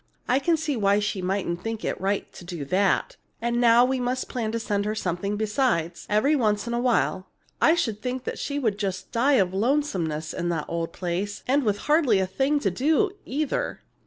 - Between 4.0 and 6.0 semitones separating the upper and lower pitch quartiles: Yes, wide, 5.4 semitones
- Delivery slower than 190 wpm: No, average, 200 wpm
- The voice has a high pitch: Yes, high, 215 Hz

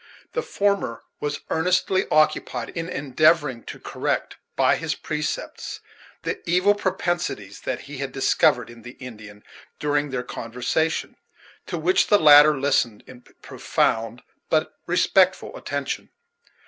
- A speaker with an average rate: No, slow, 125 wpm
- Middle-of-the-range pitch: Yes, medium, 145 Hz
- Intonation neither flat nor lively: No, wide, 5.9 semitones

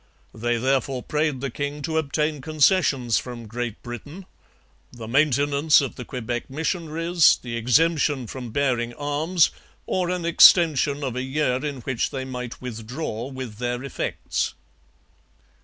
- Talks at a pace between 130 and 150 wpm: Yes, average, 140 wpm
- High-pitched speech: No, low, 135 Hz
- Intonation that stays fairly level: No, average, 3.8 semitones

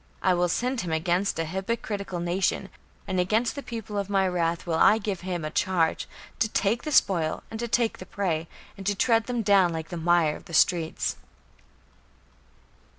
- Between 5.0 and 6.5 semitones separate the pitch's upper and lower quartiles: No, average, 4.1 semitones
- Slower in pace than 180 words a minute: No, average, 190 wpm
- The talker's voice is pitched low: No, high, 190 Hz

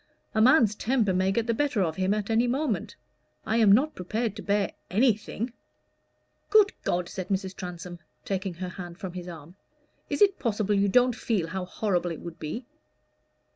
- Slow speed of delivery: No, average, 180 wpm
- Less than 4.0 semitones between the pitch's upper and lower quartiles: No, average, 4.3 semitones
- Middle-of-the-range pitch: No, high, 200 Hz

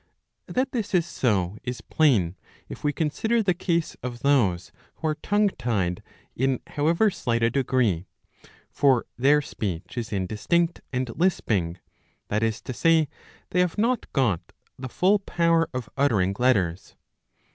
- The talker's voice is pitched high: No, low, 130 Hz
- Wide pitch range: Yes, wide, 7.7 semitones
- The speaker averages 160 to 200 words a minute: No, average, 145 wpm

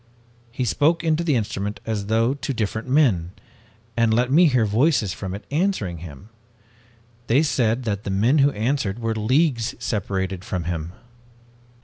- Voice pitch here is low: Yes, low, 115 Hz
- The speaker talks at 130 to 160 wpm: Yes, average, 155 wpm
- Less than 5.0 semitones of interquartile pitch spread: No, wide, 5.5 semitones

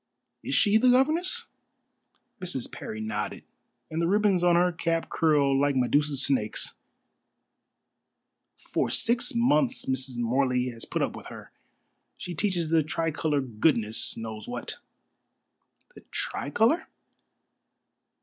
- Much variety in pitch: Yes, wide, 6.8 semitones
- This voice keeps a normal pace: No, slow, 120 wpm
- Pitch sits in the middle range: Yes, medium, 155 Hz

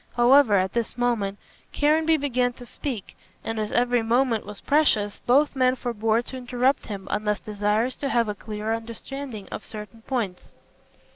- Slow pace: No, average, 160 wpm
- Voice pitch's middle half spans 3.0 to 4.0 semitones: Yes, average, 3.4 semitones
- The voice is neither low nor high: No, high, 235 Hz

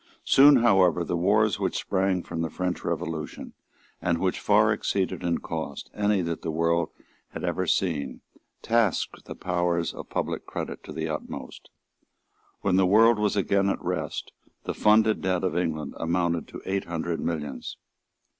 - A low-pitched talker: Yes, very low, 90 Hz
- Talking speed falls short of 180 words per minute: Yes, average, 160 wpm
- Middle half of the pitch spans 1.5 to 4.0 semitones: Yes, average, 3.2 semitones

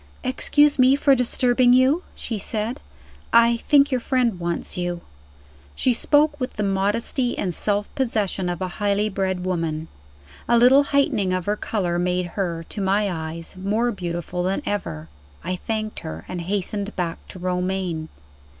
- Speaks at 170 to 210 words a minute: No, average, 160 wpm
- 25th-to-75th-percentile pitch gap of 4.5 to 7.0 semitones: Yes, average, 5.1 semitones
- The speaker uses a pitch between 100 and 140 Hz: No, high, 200 Hz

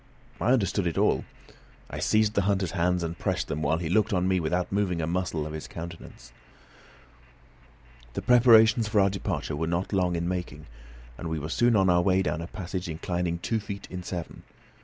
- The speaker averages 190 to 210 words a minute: Yes, average, 200 wpm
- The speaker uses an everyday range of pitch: Yes, average, 3.1 semitones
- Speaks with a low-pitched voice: Yes, very low, 90 Hz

